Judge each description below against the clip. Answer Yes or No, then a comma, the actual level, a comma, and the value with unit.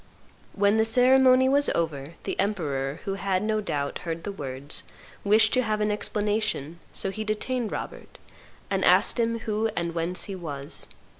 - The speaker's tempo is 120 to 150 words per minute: No, average, 165 wpm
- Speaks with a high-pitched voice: Yes, high, 205 Hz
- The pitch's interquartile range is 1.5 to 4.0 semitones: No, average, 5.0 semitones